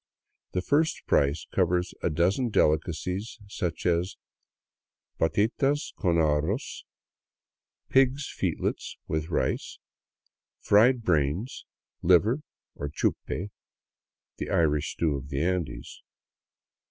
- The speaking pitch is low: Yes, very low, 90 Hz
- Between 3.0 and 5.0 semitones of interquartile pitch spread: No, wide, 5.6 semitones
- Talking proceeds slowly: Yes, slow, 105 wpm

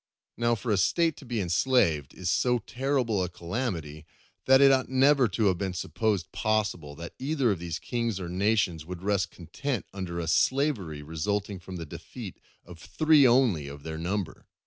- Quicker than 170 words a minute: Yes, average, 180 wpm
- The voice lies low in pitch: Yes, low, 100 Hz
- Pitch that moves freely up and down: Yes, wide, 6.4 semitones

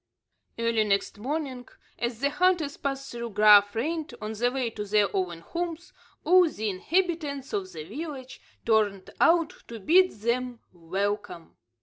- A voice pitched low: No, high, 235 Hz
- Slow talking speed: No, average, 145 wpm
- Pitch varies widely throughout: Yes, wide, 6.6 semitones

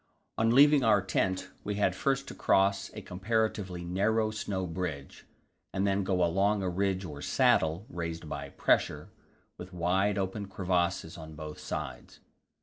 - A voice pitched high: No, very low, 95 Hz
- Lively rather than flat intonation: No, average, 2.8 semitones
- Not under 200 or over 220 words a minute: No, average, 150 wpm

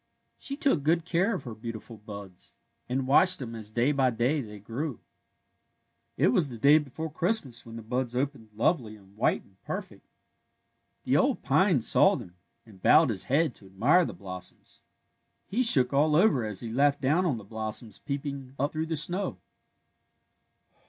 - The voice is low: Yes, low, 130 Hz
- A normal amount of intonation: No, wide, 5.8 semitones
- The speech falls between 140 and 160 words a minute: No, average, 175 wpm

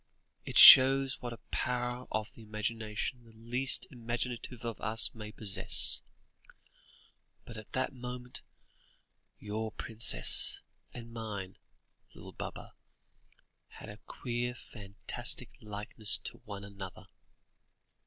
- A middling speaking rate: No, slow, 105 wpm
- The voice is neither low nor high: No, low, 115 Hz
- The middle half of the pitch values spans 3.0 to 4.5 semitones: No, narrow, 2.5 semitones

